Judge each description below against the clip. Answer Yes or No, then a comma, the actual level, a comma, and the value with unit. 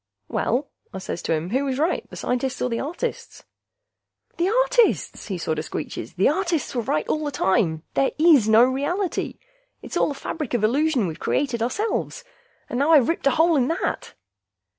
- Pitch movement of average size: No, wide, 6.0 semitones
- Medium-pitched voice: No, very high, 275 Hz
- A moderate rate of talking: Yes, average, 185 wpm